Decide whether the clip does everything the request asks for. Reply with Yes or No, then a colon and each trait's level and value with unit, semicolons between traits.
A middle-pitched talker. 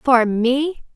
No: very high, 255 Hz